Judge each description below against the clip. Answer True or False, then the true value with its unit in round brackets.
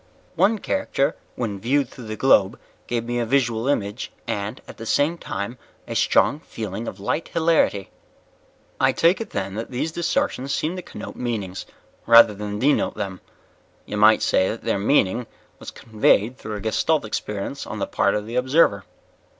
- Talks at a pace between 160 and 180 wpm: True (175 wpm)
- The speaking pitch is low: True (115 Hz)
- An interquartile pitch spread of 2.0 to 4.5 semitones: False (5.2 semitones)